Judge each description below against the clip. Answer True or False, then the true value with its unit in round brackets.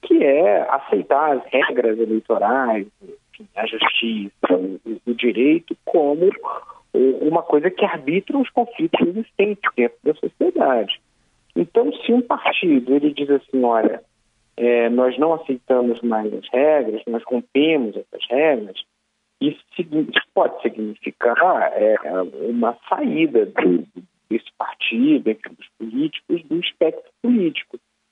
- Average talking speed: False (115 wpm)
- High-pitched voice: False (155 Hz)